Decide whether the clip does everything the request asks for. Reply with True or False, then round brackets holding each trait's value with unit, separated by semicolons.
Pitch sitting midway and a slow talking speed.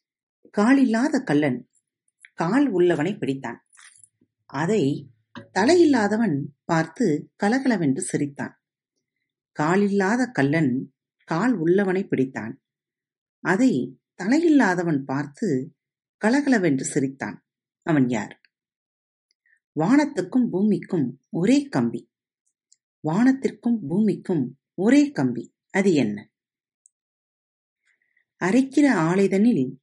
True (180 Hz; 65 wpm)